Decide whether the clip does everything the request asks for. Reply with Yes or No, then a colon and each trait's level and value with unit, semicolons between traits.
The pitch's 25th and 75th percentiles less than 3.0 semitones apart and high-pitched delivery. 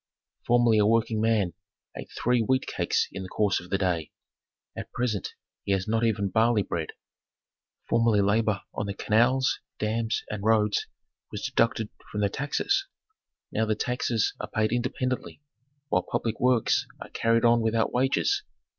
No: narrow, 2.4 semitones; low, 110 Hz